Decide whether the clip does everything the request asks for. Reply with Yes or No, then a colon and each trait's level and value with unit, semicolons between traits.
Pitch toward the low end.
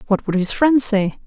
No: high, 215 Hz